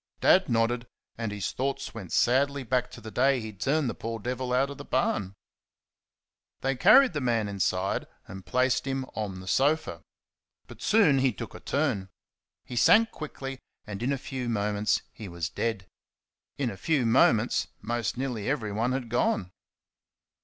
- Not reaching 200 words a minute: Yes, average, 165 wpm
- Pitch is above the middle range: No, low, 120 Hz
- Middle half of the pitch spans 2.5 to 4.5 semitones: Yes, average, 4.2 semitones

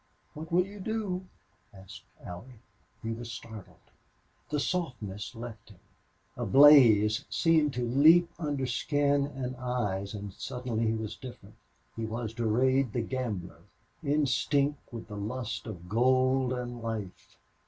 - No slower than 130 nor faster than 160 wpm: Yes, slow, 135 wpm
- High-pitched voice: No, low, 125 Hz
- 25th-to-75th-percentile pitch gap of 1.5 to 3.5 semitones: No, average, 4.2 semitones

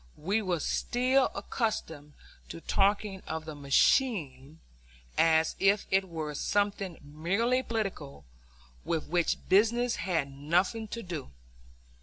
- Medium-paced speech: No, slow, 115 wpm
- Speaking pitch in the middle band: Yes, medium, 180 Hz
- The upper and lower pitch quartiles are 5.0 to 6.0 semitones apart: Yes, wide, 5.6 semitones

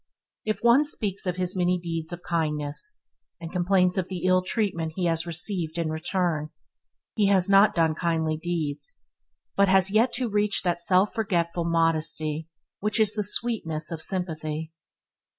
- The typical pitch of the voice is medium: Yes, medium, 175 Hz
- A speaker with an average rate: Yes, average, 160 wpm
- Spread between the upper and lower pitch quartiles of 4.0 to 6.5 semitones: No, average, 3.3 semitones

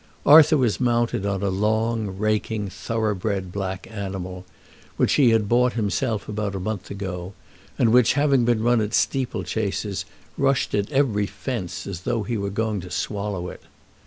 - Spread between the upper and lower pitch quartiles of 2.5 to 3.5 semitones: Yes, average, 3.2 semitones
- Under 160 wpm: No, average, 165 wpm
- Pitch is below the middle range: Yes, low, 105 Hz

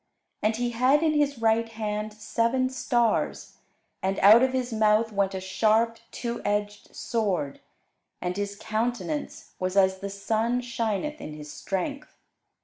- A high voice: Yes, high, 220 Hz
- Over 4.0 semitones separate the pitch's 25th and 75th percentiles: No, average, 3.2 semitones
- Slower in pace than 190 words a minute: Yes, average, 145 wpm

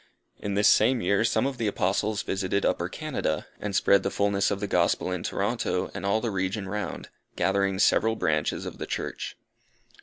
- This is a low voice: Yes, low, 100 Hz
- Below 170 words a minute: No, average, 185 wpm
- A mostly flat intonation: Yes, narrow, 2.1 semitones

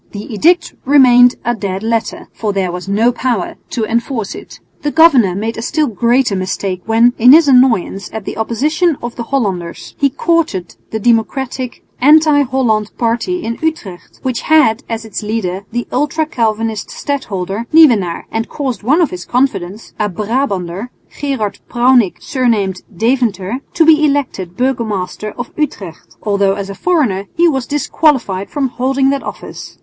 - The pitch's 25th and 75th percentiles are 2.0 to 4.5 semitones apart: No, average, 5.2 semitones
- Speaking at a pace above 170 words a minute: No, average, 160 wpm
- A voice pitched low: No, high, 235 Hz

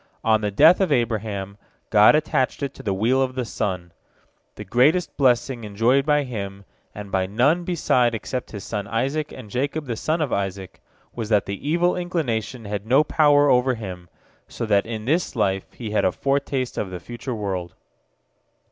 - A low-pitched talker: Yes, low, 120 Hz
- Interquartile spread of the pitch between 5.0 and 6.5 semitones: Yes, wide, 5.5 semitones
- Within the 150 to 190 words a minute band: Yes, average, 185 wpm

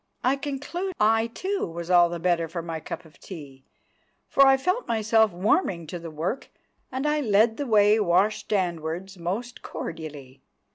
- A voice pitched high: Yes, high, 200 Hz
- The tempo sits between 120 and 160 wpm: Yes, average, 155 wpm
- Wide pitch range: Yes, wide, 6.3 semitones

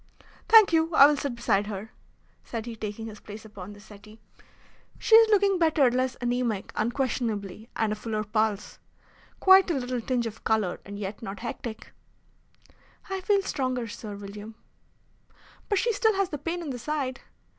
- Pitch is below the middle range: No, high, 235 Hz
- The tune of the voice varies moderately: No, wide, 6.0 semitones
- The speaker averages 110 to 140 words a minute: No, average, 170 wpm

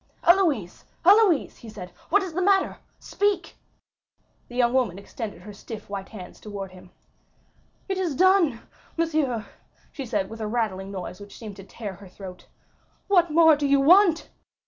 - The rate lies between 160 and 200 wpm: Yes, average, 165 wpm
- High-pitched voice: Yes, high, 240 Hz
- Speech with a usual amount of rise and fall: No, wide, 9.0 semitones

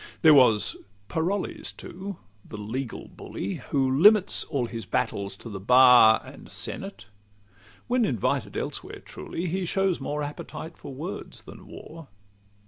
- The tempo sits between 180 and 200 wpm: No, average, 140 wpm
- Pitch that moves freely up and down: Yes, wide, 7.3 semitones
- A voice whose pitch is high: No, medium, 140 Hz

